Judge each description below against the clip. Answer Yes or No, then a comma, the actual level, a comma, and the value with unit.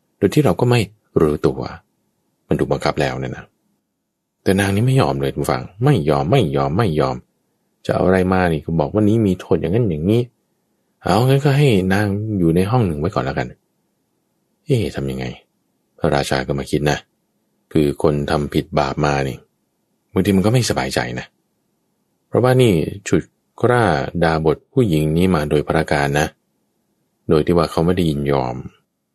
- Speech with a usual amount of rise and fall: No, wide, 5.7 semitones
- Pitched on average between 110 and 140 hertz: No, very low, 80 Hz